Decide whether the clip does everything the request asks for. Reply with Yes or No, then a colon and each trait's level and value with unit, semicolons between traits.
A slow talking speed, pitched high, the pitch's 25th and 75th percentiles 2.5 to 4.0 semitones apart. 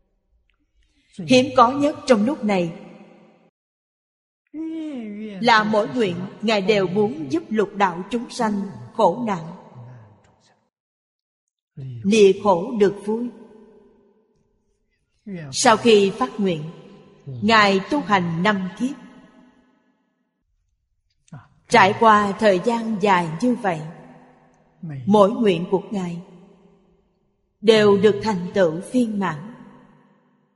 Yes: slow, 95 wpm; high, 205 Hz; average, 3.4 semitones